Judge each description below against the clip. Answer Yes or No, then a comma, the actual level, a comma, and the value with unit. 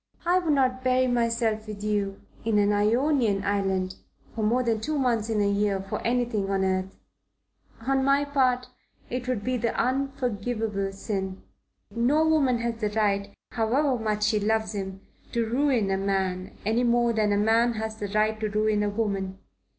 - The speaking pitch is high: Yes, high, 220 Hz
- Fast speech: No, average, 175 wpm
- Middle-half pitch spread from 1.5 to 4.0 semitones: Yes, average, 3.5 semitones